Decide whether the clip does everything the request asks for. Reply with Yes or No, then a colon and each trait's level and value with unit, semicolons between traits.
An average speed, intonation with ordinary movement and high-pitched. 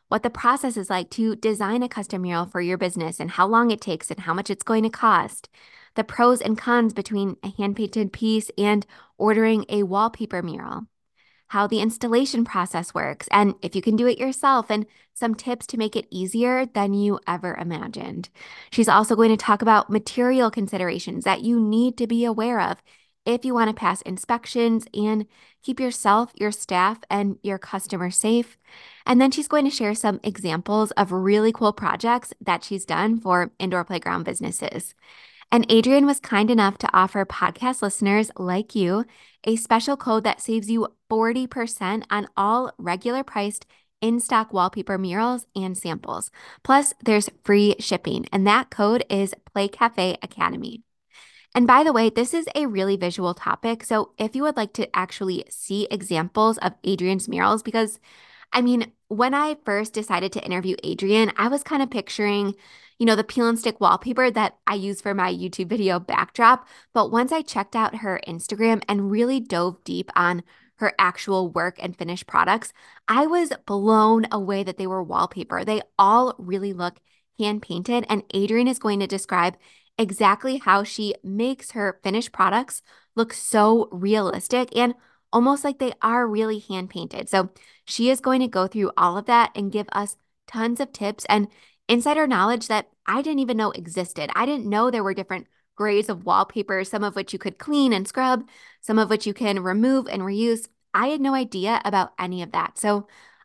Yes: average, 185 wpm; average, 3.1 semitones; high, 215 Hz